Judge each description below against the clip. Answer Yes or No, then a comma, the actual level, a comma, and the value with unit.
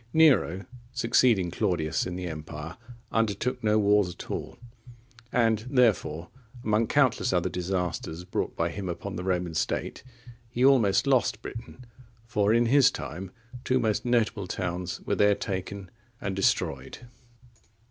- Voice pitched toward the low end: Yes, low, 100 Hz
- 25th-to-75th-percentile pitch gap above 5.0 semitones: No, average, 4.7 semitones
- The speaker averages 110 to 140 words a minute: Yes, slow, 135 wpm